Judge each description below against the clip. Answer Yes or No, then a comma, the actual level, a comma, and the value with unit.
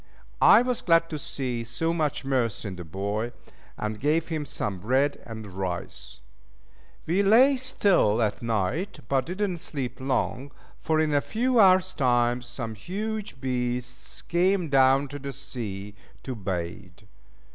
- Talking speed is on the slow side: No, average, 150 wpm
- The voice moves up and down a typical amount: No, wide, 6.9 semitones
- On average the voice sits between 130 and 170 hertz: Yes, low, 135 Hz